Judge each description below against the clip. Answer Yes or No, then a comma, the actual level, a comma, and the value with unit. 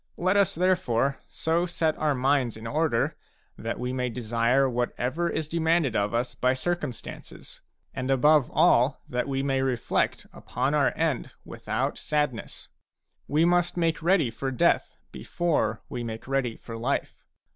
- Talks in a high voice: No, low, 135 Hz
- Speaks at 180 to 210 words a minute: No, average, 155 wpm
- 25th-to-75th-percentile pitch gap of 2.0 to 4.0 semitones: No, average, 4.7 semitones